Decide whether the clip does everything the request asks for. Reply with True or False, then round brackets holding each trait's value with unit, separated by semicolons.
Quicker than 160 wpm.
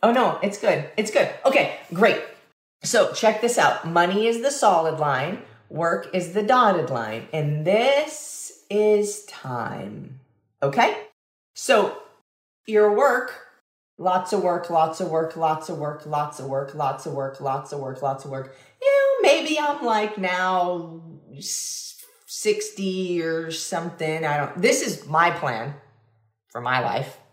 False (150 wpm)